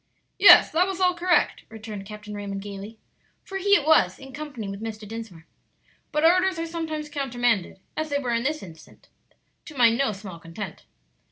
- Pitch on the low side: No, high, 240 Hz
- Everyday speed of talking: Yes, average, 180 wpm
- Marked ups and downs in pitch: Yes, wide, 7.3 semitones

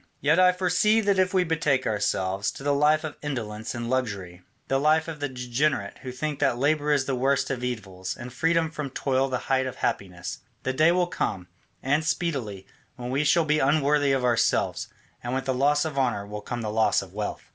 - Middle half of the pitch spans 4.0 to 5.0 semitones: Yes, average, 4.3 semitones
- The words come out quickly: Yes, fast, 210 wpm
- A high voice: No, low, 135 Hz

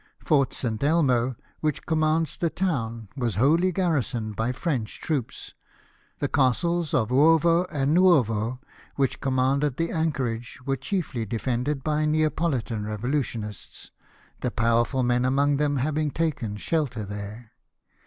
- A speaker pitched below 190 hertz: Yes, low, 135 Hz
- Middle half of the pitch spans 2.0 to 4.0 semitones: No, average, 4.9 semitones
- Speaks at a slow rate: Yes, slow, 130 wpm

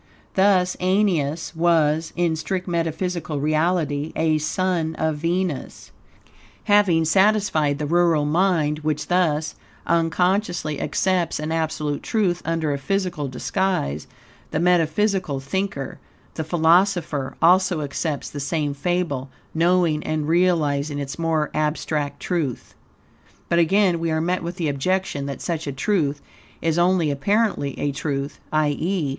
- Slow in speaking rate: Yes, slow, 125 wpm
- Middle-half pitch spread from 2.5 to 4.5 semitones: Yes, average, 3.3 semitones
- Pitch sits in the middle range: Yes, medium, 165 Hz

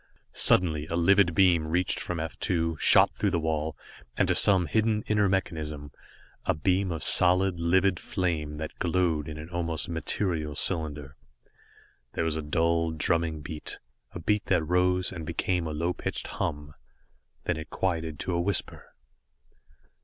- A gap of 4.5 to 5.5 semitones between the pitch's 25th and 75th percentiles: No, average, 2.7 semitones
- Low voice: Yes, very low, 85 Hz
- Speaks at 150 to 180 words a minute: Yes, average, 160 wpm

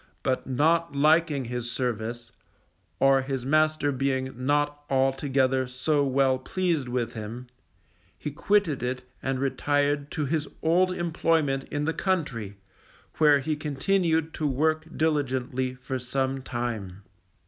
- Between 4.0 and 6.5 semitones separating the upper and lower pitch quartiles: No, average, 3.3 semitones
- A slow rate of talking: Yes, slow, 125 wpm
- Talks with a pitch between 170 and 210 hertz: No, low, 135 Hz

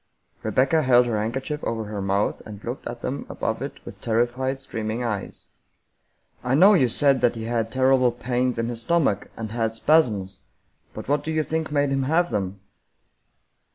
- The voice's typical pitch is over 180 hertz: No, low, 120 Hz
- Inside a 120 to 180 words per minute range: No, average, 190 wpm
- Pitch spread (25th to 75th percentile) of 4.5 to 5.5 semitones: No, average, 3.6 semitones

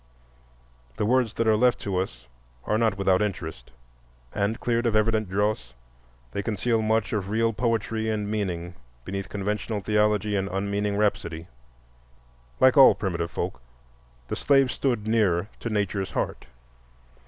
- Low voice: Yes, low, 105 Hz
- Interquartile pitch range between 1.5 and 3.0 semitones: Yes, narrow, 2.5 semitones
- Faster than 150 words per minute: No, average, 140 wpm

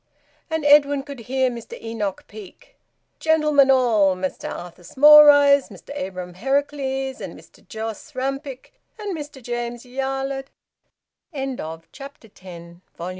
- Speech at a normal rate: No, slow, 125 wpm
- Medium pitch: No, very high, 265 Hz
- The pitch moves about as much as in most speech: Yes, average, 4.5 semitones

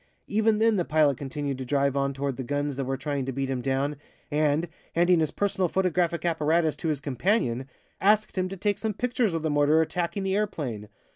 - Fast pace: Yes, fast, 210 wpm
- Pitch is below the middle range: No, medium, 155 Hz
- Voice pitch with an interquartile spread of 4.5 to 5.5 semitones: Yes, average, 5.1 semitones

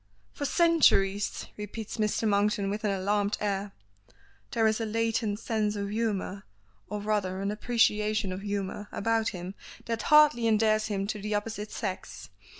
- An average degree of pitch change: No, narrow, 1.8 semitones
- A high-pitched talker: Yes, high, 210 Hz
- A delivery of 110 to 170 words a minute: Yes, average, 150 wpm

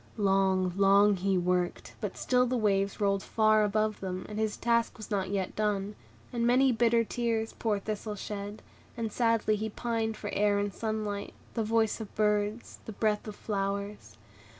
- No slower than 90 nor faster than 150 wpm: No, average, 175 wpm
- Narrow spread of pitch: Yes, narrow, 2.0 semitones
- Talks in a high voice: Yes, high, 210 Hz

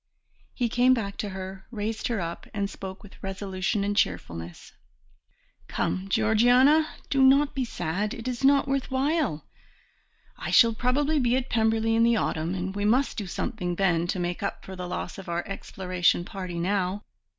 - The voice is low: No, high, 205 Hz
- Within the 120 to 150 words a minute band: No, average, 175 wpm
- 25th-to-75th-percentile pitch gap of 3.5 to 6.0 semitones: Yes, average, 4.9 semitones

